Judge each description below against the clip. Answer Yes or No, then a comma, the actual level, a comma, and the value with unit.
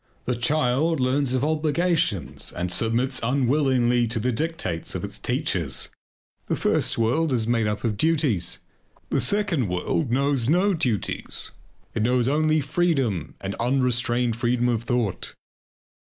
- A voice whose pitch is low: Yes, low, 125 Hz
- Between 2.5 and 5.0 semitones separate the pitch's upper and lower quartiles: Yes, average, 4.6 semitones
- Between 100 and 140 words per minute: Yes, slow, 135 wpm